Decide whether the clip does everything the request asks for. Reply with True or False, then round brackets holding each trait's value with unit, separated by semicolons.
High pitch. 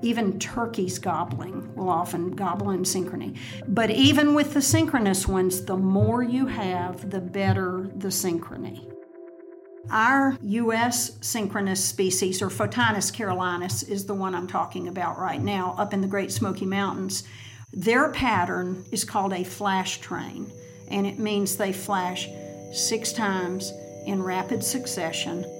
True (195 Hz)